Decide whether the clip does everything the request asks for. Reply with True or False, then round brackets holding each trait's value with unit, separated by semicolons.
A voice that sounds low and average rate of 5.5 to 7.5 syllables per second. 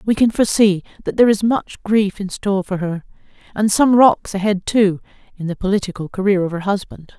False (200 Hz; 5.7 syllables/s)